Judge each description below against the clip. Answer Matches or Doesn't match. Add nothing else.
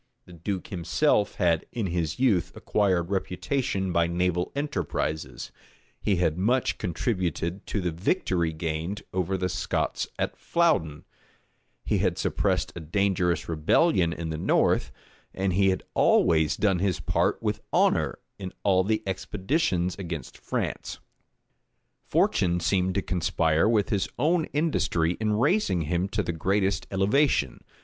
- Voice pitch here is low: Matches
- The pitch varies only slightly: Doesn't match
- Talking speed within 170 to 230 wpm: Doesn't match